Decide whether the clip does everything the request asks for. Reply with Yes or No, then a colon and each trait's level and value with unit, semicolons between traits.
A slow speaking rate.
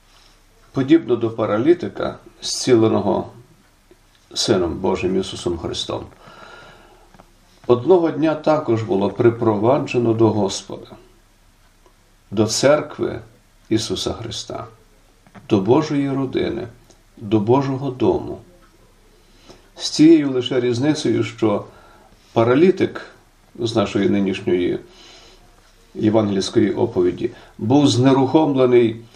Yes: slow, 80 wpm